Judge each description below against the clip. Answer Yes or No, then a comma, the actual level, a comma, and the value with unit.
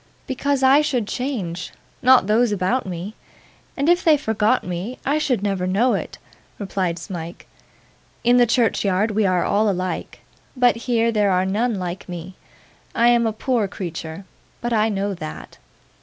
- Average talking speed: Yes, average, 160 wpm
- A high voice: Yes, high, 210 Hz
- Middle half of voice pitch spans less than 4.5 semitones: No, average, 4.9 semitones